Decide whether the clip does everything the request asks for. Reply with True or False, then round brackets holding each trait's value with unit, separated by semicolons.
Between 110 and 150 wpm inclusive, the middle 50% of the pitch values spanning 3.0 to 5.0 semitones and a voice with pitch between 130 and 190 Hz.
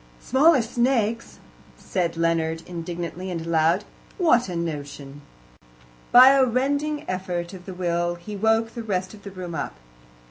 False (145 wpm; 5.5 semitones; 185 Hz)